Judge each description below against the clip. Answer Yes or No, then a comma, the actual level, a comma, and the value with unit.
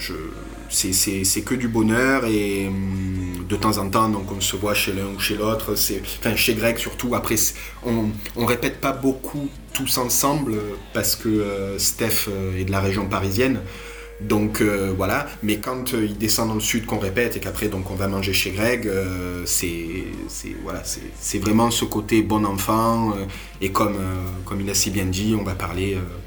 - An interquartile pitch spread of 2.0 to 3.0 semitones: Yes, narrow, 2.6 semitones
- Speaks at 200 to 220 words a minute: Yes, average, 210 wpm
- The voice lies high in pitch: No, low, 105 Hz